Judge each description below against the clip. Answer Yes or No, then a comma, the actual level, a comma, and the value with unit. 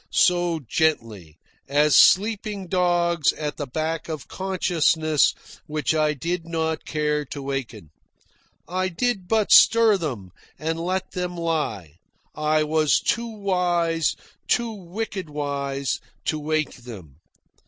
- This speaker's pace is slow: Yes, slow, 120 wpm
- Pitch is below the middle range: No, medium, 160 Hz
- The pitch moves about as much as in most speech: Yes, average, 3.6 semitones